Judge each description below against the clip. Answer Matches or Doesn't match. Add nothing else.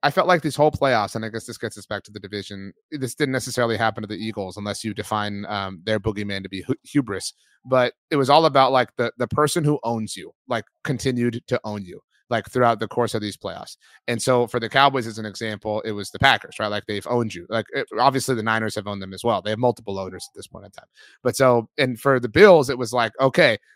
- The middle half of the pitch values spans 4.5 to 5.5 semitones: Doesn't match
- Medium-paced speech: Doesn't match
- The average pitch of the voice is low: Matches